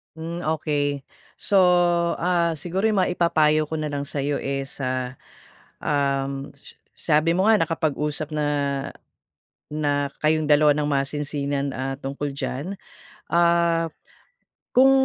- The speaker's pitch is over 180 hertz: No, medium, 150 Hz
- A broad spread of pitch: No, average, 2.9 semitones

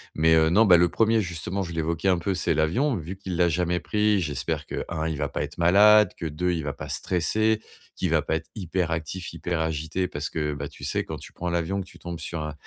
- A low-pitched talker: Yes, very low, 85 Hz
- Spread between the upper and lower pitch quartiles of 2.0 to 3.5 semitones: Yes, average, 2.9 semitones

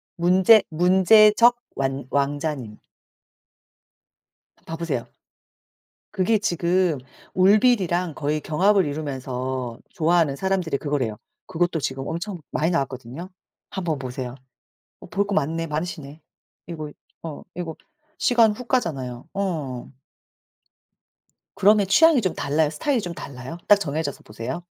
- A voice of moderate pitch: Yes, medium, 165 Hz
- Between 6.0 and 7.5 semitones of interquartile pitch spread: No, wide, 5.4 semitones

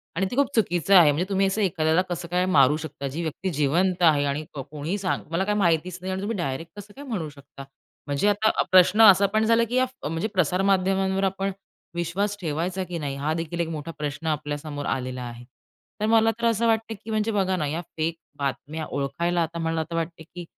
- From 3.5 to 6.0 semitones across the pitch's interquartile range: Yes, average, 4.2 semitones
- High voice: No, medium, 170 Hz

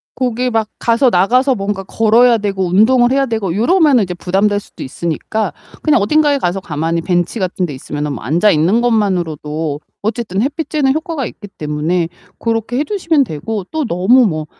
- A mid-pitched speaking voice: No, high, 210 Hz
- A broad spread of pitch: Yes, wide, 6.1 semitones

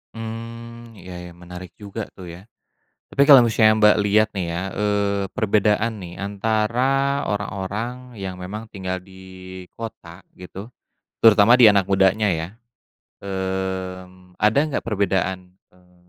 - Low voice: Yes, low, 100 Hz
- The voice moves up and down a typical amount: Yes, average, 3.3 semitones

